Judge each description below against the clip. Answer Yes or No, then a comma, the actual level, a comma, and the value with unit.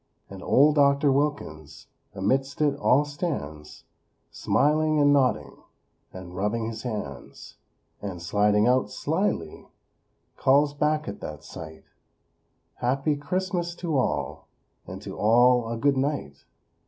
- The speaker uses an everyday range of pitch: No, wide, 6.0 semitones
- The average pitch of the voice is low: Yes, low, 130 Hz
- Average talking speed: No, slow, 120 wpm